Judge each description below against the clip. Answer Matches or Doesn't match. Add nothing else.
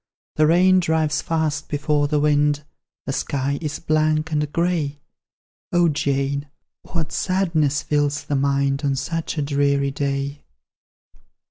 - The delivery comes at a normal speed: Doesn't match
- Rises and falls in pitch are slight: Matches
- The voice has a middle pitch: Matches